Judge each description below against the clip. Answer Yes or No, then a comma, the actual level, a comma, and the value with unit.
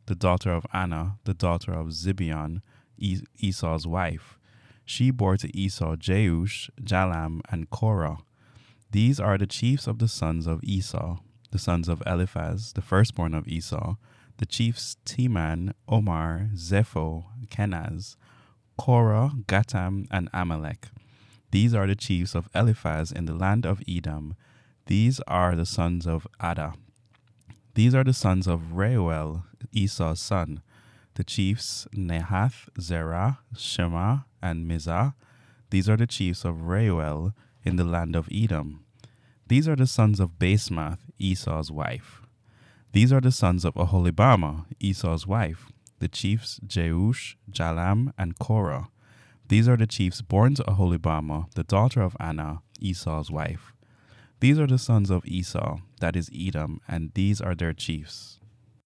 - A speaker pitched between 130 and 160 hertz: No, low, 100 Hz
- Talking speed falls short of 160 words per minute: Yes, average, 140 wpm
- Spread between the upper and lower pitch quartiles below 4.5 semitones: No, average, 5.2 semitones